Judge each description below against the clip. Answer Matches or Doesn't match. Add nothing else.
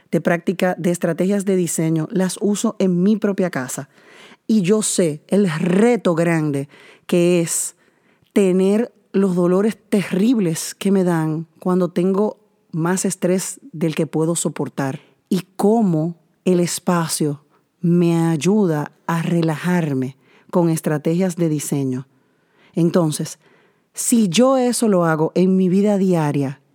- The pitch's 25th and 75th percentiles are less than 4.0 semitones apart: Matches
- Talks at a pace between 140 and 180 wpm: Doesn't match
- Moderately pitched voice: Matches